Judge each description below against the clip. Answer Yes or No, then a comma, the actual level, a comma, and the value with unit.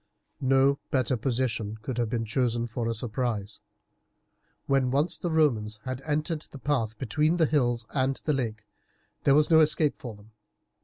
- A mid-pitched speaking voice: No, low, 130 Hz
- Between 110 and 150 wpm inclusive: No, average, 165 wpm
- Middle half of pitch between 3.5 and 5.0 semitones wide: Yes, average, 4.2 semitones